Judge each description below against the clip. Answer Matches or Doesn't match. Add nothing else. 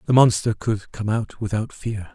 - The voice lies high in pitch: Doesn't match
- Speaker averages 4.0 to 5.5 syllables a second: Matches